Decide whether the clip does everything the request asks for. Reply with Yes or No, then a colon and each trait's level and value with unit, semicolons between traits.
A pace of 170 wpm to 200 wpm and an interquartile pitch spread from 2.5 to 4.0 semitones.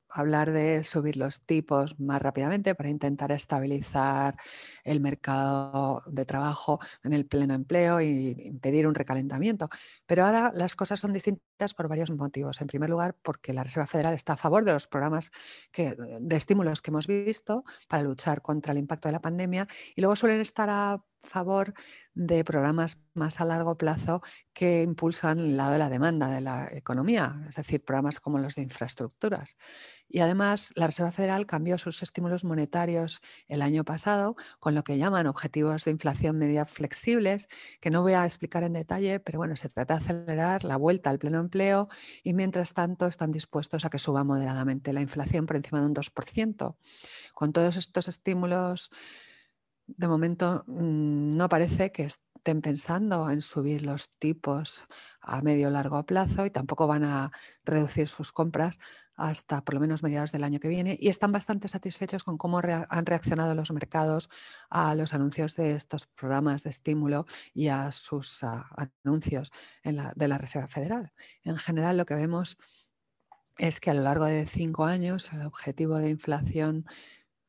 Yes: average, 175 wpm; average, 3.3 semitones